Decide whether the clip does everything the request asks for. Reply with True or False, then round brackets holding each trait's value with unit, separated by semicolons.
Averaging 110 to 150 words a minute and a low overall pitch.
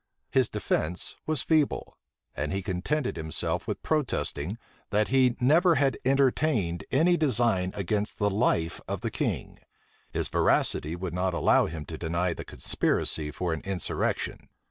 True (145 wpm; 100 Hz)